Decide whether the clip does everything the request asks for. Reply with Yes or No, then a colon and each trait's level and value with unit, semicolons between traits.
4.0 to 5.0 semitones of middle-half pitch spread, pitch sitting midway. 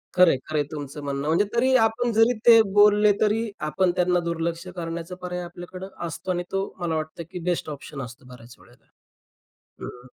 Yes: average, 4.6 semitones; medium, 175 Hz